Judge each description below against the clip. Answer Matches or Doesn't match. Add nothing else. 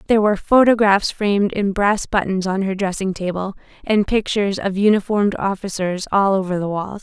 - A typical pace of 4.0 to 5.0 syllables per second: Doesn't match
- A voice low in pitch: Doesn't match